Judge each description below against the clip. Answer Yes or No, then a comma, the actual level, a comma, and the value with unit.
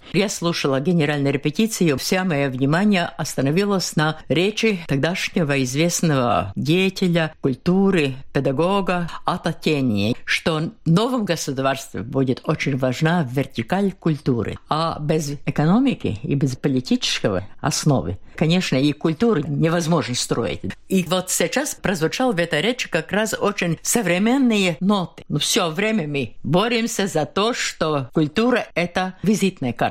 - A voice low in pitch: No, medium, 170 Hz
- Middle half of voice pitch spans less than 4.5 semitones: No, average, 5.0 semitones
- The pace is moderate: Yes, average, 125 wpm